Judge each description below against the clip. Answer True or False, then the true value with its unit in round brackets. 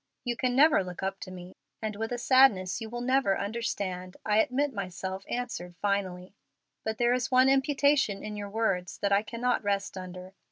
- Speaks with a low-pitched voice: False (210 Hz)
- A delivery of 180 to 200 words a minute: True (190 wpm)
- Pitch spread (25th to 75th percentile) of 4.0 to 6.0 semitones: True (4.7 semitones)